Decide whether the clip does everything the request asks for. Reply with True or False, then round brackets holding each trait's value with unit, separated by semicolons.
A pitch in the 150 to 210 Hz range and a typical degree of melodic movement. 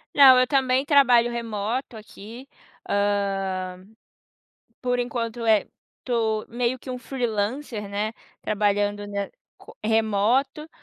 False (225 Hz; 3.6 semitones)